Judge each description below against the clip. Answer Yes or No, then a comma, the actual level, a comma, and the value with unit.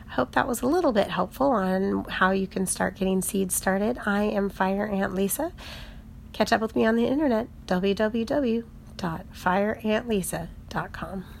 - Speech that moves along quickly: No, average, 155 wpm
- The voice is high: Yes, high, 205 Hz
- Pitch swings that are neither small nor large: Yes, average, 3.2 semitones